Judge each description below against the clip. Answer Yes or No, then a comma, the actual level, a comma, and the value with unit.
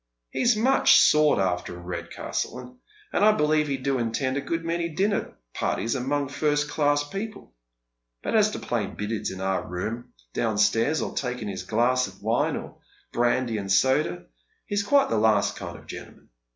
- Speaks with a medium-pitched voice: No, low, 130 Hz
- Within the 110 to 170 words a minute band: No, average, 180 wpm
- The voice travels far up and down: Yes, wide, 6.3 semitones